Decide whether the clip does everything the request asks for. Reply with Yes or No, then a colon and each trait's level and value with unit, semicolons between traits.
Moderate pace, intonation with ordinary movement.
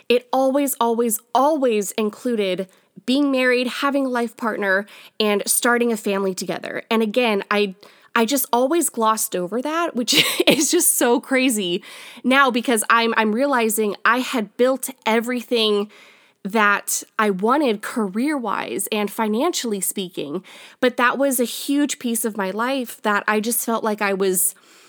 Yes: average, 150 wpm; average, 3.7 semitones